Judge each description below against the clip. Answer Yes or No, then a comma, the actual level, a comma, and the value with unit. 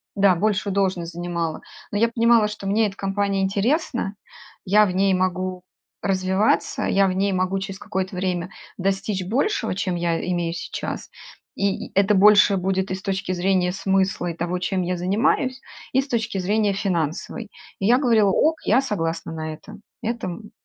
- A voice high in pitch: Yes, high, 195 Hz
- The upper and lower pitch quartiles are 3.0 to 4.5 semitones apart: No, narrow, 2.4 semitones